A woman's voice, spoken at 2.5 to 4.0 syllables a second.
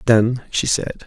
No: male; 3.5 syllables/s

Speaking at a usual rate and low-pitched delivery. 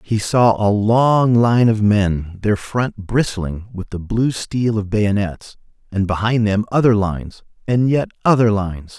Yes: average, 165 wpm; low, 105 Hz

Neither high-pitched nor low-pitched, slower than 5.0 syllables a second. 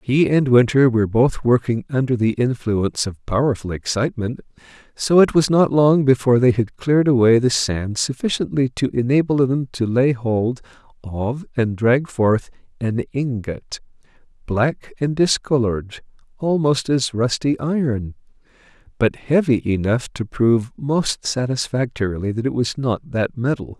No: low, 125 Hz; 4.6 syllables/s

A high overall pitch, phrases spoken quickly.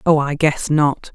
No: medium, 150 Hz; fast, 210 wpm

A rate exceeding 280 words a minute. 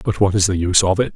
Yes: fast, 365 wpm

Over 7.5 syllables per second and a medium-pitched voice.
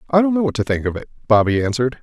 No: 7.9 syllables/s; low, 130 Hz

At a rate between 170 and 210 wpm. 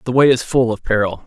No: fast, 285 wpm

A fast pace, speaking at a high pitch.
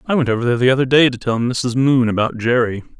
No: fast, 260 wpm; low, 125 Hz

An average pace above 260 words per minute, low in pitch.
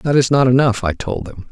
Yes: fast, 275 wpm; low, 120 Hz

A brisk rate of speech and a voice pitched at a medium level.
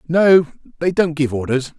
No: average, 170 wpm; medium, 160 Hz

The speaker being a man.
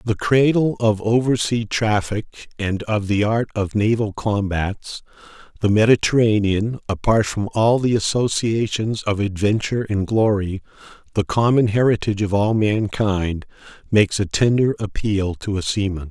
Yes: male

